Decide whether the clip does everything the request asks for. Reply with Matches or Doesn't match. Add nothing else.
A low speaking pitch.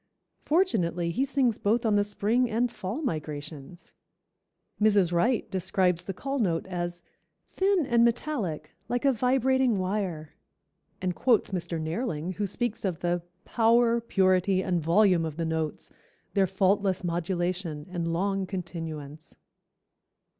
Doesn't match